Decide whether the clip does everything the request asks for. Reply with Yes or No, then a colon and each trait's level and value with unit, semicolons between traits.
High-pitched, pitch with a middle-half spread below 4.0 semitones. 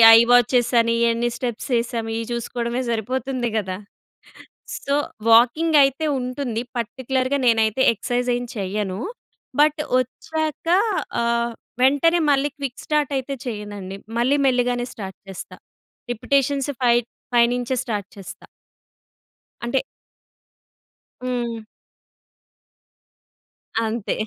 Yes: high, 245 Hz; average, 2.8 semitones